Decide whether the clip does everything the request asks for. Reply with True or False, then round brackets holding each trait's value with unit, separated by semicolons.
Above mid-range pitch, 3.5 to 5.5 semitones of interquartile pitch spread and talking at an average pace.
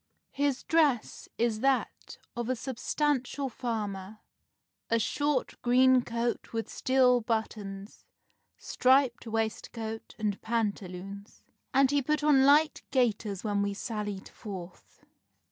False (235 Hz; 3.9 semitones; 110 wpm)